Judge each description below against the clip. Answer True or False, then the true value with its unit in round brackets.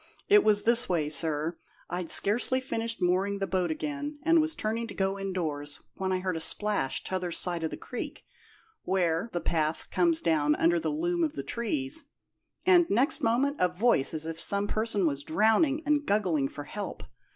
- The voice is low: False (195 Hz)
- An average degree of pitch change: False (6.7 semitones)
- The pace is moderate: True (185 wpm)